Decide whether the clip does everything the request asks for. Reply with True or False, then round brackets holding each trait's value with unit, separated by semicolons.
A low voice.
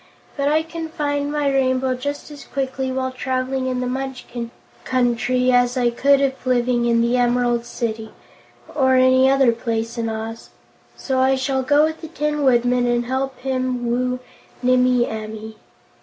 False (255 Hz)